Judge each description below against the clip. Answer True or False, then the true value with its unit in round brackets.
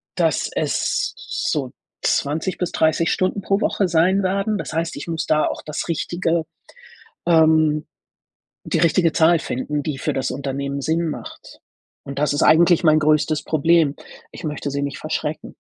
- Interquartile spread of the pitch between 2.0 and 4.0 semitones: True (2.4 semitones)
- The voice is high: False (160 Hz)